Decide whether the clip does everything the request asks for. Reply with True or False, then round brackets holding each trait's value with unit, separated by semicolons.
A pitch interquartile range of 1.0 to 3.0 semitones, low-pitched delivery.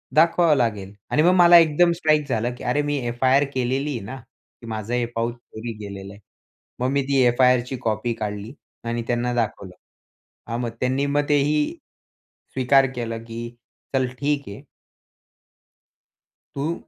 False (3.8 semitones; 125 Hz)